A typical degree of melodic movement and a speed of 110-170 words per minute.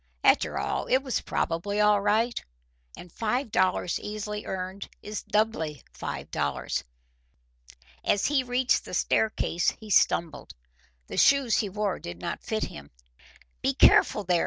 Yes: average, 3.7 semitones; average, 140 wpm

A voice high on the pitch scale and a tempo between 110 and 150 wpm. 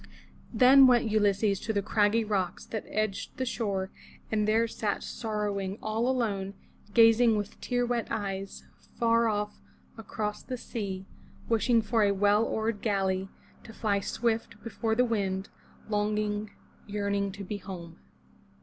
Yes: high, 210 Hz; average, 140 wpm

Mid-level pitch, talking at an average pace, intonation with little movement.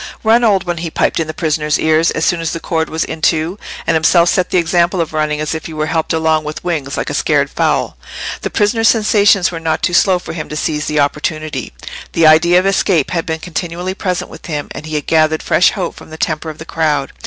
No: medium, 160 Hz; fast, 245 wpm; narrow, 2.2 semitones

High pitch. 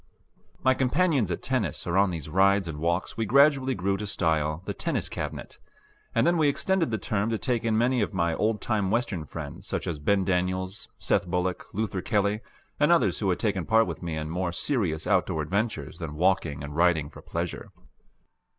No: very low, 95 Hz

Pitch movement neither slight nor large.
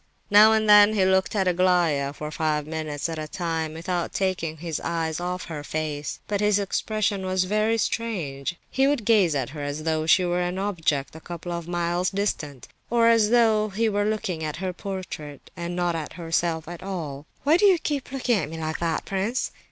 Yes: average, 4.5 semitones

